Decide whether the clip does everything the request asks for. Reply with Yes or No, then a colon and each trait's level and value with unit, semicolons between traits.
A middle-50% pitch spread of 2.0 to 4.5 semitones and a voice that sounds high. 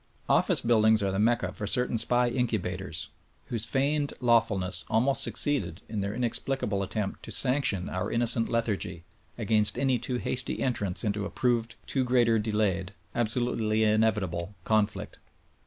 No: average, 3.3 semitones; low, 110 Hz